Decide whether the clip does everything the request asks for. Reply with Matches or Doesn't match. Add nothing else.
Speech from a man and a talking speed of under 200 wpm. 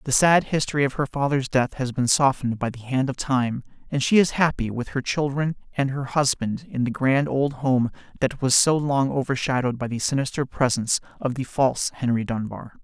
Doesn't match